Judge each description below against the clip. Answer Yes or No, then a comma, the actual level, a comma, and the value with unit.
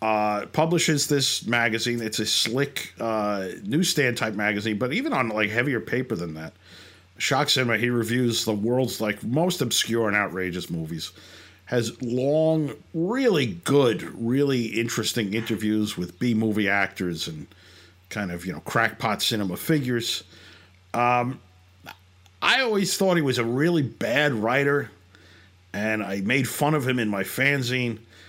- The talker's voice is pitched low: Yes, low, 115 Hz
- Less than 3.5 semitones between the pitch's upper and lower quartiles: No, wide, 5.5 semitones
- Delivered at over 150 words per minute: No, average, 145 wpm